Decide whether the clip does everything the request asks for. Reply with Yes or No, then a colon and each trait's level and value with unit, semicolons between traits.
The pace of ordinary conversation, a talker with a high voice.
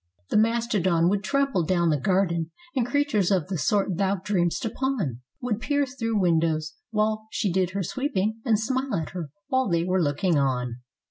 Yes: average, 180 wpm; high, 195 Hz